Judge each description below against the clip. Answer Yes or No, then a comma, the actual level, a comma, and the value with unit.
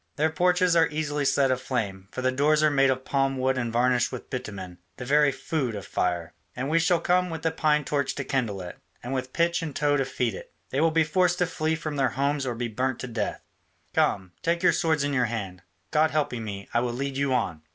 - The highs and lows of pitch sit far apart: No, average, 4.3 semitones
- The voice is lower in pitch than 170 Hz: Yes, low, 135 Hz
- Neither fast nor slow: No, fast, 240 wpm